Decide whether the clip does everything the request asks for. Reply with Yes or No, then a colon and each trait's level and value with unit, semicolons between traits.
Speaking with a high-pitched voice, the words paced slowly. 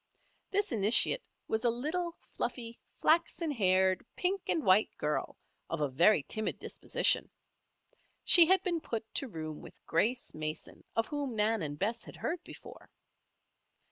No: high, 225 Hz; average, 145 wpm